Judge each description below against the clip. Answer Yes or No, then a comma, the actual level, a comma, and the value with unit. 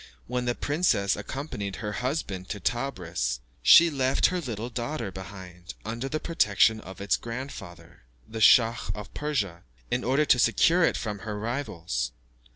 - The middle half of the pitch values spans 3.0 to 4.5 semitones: No, wide, 5.4 semitones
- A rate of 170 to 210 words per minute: No, average, 155 wpm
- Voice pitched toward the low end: Yes, low, 115 Hz